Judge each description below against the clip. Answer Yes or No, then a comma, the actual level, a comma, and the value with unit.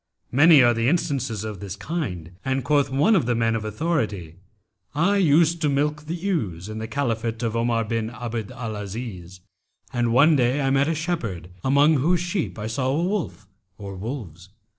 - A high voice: No, low, 125 Hz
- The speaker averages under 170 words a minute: No, average, 185 wpm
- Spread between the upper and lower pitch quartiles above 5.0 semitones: Yes, wide, 5.6 semitones